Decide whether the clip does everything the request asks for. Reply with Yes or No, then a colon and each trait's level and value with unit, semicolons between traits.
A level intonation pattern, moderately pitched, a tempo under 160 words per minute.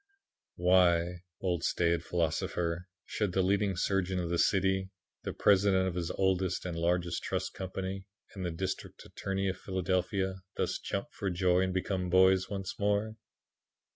No: narrow, 1.5 semitones; very low, 95 Hz; average, 150 wpm